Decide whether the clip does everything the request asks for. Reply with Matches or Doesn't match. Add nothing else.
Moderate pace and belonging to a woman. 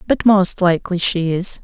Matches